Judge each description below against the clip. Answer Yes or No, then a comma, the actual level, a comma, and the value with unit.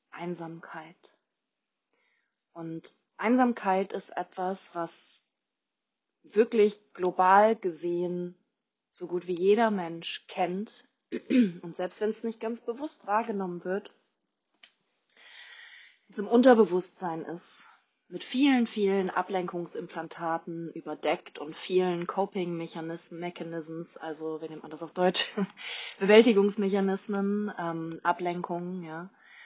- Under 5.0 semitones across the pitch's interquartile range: Yes, average, 3.6 semitones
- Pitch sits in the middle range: Yes, medium, 180 Hz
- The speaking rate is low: Yes, slow, 95 wpm